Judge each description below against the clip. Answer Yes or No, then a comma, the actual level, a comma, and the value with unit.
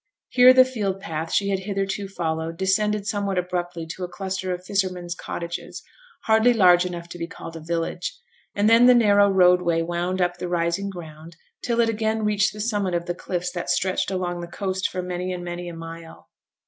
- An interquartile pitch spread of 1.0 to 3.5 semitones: Yes, narrow, 2.6 semitones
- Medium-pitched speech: Yes, medium, 180 Hz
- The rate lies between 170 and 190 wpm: No, average, 200 wpm